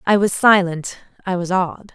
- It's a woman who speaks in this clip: Yes, female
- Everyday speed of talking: Yes, average, 185 wpm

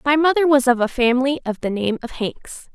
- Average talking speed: No, fast, 240 wpm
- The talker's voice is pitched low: No, very high, 260 Hz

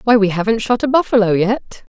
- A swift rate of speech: Yes, fast, 210 wpm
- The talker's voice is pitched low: No, high, 220 Hz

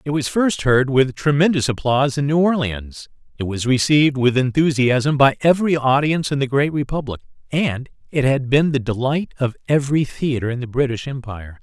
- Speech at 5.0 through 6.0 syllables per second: Yes, 5.4 syllables/s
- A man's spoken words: Yes, male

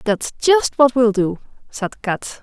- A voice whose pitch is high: Yes, high, 240 Hz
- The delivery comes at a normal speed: Yes, average, 175 wpm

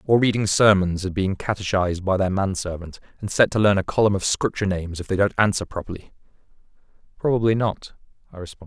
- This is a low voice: Yes, low, 100 Hz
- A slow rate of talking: No, average, 185 wpm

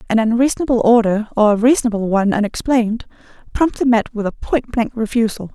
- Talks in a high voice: Yes, high, 225 Hz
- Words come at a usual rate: Yes, average, 160 wpm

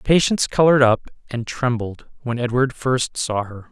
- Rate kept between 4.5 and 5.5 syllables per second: Yes, 5.0 syllables/s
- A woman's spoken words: No, male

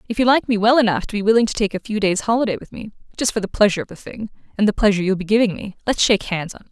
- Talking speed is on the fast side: Yes, fast, 320 wpm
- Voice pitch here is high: Yes, high, 210 Hz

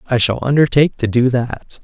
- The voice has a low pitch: Yes, low, 125 Hz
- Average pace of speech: Yes, average, 195 wpm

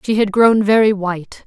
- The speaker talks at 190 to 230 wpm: Yes, fast, 205 wpm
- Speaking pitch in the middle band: No, high, 205 Hz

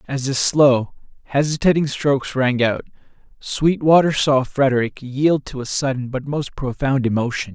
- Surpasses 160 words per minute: No, average, 145 wpm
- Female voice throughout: No, male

